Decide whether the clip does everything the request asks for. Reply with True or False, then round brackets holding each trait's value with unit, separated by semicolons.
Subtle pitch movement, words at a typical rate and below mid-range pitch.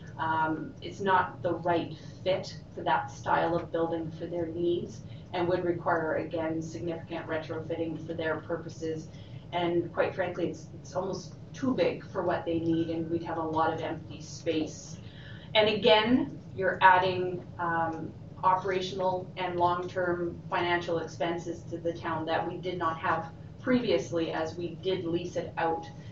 False (1.9 semitones; 160 wpm; 165 Hz)